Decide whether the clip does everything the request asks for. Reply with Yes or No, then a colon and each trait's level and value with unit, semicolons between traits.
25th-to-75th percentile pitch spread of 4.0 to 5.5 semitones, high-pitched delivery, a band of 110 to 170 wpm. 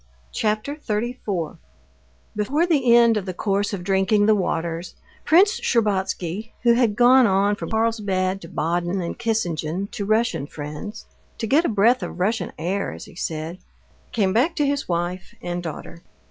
Yes: average, 4.7 semitones; high, 205 Hz; average, 155 wpm